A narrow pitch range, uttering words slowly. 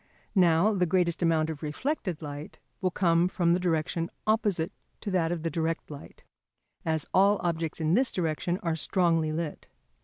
No: narrow, 2.3 semitones; average, 165 wpm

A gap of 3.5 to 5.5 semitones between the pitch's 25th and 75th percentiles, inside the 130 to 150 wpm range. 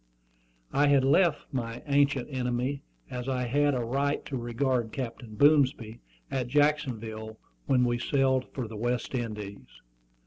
No: average, 3.1 semitones; average, 140 wpm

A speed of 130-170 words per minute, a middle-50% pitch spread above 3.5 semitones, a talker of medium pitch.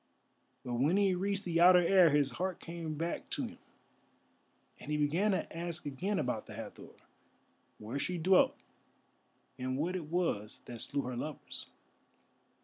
Yes: average, 150 wpm; average, 4.5 semitones; medium, 165 Hz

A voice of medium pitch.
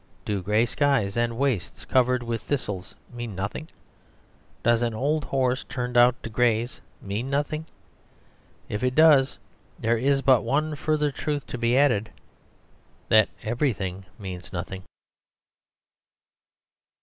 No: low, 120 Hz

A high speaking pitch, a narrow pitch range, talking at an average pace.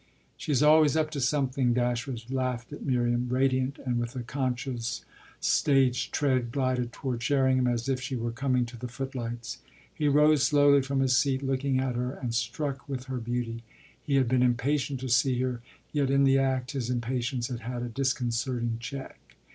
No: low, 130 Hz; narrow, 2.0 semitones; average, 180 wpm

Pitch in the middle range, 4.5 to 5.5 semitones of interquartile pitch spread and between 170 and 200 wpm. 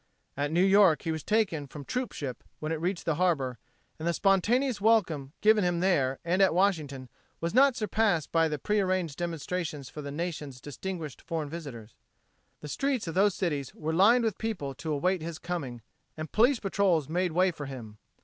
Yes: medium, 170 Hz; average, 4.9 semitones; average, 190 wpm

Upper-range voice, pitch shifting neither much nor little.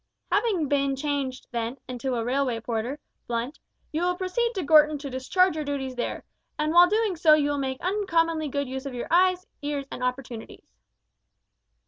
Yes: very high, 285 Hz; average, 4.8 semitones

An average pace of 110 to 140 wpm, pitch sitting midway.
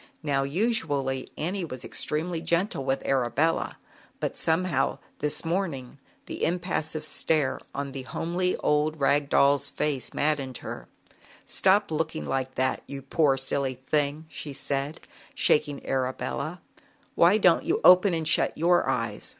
Yes: slow, 135 wpm; medium, 150 Hz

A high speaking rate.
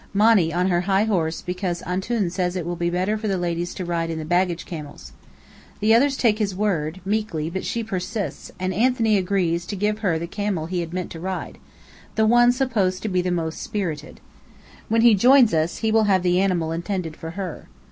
Yes: fast, 210 wpm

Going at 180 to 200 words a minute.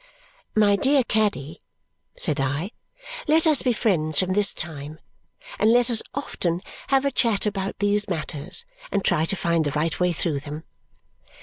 No: average, 165 wpm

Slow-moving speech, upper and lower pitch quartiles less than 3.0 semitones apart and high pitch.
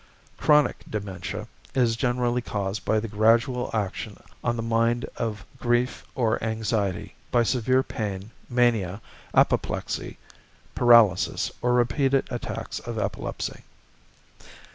No: slow, 110 wpm; narrow, 2.4 semitones; low, 115 Hz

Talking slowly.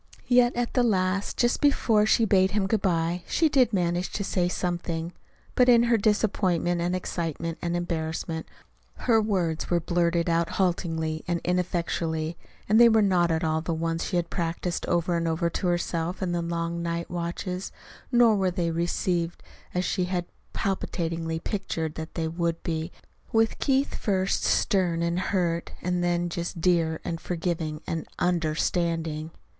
No: average, 165 wpm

